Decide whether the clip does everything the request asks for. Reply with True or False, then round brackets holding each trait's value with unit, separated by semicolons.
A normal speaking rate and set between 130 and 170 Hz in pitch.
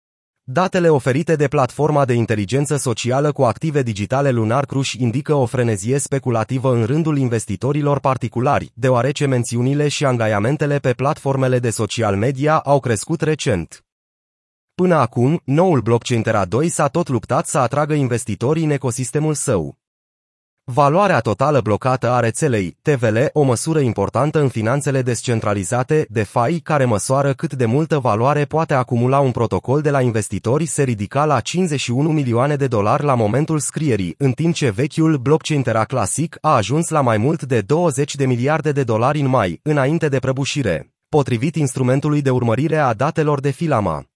True (155 wpm; 135 Hz)